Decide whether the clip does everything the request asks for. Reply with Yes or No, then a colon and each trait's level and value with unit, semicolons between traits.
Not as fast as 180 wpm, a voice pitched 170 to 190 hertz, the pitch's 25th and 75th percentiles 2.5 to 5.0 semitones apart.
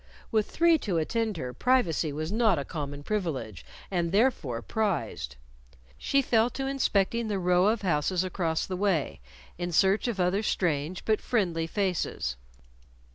No: average, 150 wpm; medium, 185 Hz; wide, 5.4 semitones